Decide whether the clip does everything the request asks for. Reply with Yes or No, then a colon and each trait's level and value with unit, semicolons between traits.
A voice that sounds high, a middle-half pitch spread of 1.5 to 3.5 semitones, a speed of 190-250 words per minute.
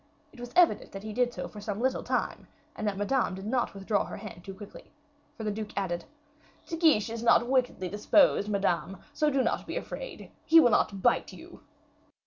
No: high, 215 Hz; average, 4.2 semitones; fast, 205 wpm